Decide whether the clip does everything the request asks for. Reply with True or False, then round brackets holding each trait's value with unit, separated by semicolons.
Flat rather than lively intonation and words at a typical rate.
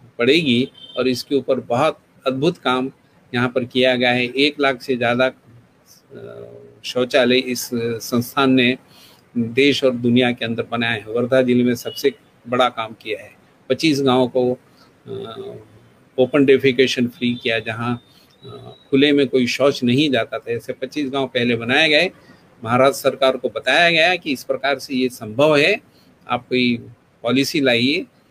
False (1.9 semitones; 155 wpm)